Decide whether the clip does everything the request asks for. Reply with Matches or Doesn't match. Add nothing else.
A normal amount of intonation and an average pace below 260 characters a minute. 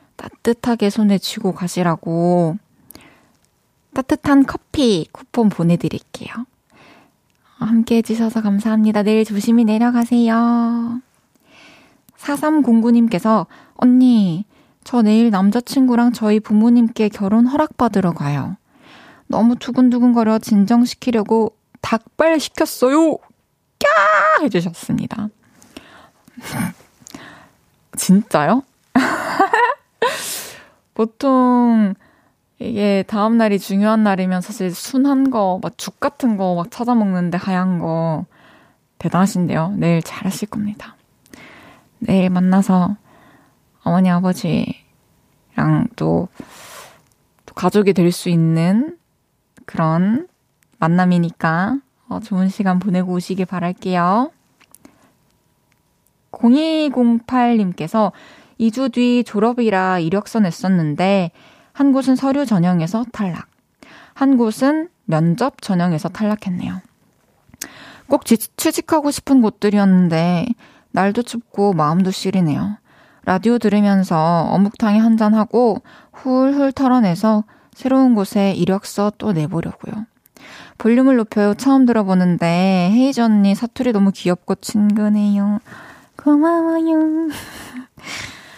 Matches